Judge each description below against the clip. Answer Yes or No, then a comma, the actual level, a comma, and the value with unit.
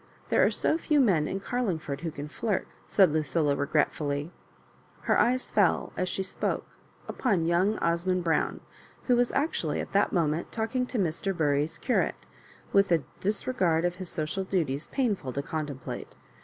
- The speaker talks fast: No, average, 170 wpm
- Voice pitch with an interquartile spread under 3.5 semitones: No, average, 5.0 semitones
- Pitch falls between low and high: Yes, medium, 175 Hz